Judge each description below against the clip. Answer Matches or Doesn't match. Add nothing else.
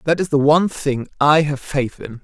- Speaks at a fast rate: Matches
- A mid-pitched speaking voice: Matches